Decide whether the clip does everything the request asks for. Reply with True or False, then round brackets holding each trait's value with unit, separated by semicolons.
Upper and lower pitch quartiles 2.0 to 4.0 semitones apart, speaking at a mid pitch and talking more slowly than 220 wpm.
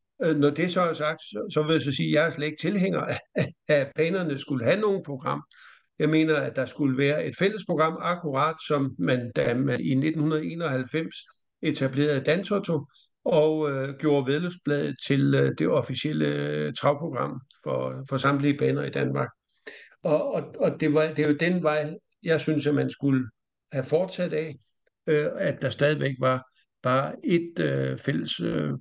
True (2.8 semitones; 150 Hz; 175 wpm)